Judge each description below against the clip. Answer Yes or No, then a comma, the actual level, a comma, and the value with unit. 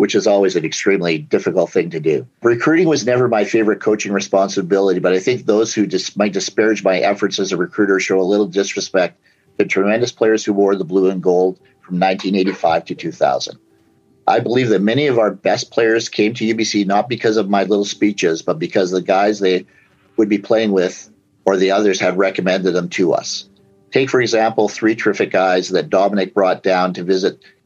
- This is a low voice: Yes, low, 100 Hz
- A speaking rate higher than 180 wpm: Yes, fast, 205 wpm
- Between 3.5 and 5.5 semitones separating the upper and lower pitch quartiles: No, narrow, 2.4 semitones